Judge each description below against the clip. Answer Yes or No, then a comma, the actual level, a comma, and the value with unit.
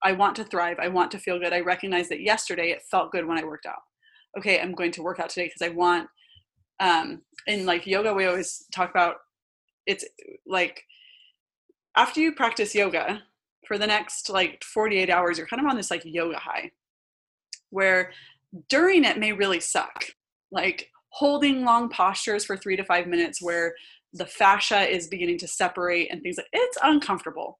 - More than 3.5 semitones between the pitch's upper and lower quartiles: Yes, average, 4.2 semitones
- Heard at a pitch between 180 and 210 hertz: Yes, high, 190 Hz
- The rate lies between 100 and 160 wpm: No, average, 185 wpm